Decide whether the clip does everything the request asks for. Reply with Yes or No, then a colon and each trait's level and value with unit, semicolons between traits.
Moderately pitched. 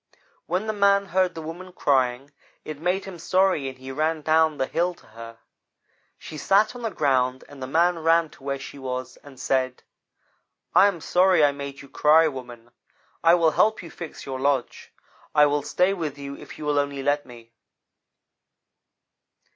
Yes: medium, 150 Hz